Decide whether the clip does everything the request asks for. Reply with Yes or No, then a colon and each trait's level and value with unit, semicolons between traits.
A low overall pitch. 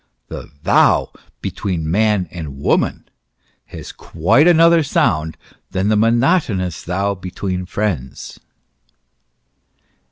Yes: very low, 95 Hz